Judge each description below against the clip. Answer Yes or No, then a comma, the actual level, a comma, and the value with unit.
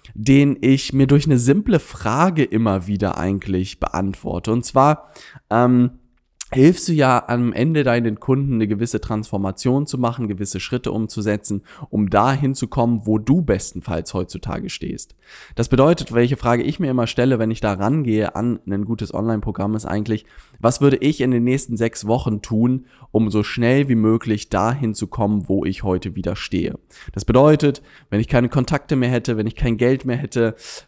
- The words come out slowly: No, average, 180 wpm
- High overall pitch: No, low, 115 Hz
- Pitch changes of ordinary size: Yes, average, 3.7 semitones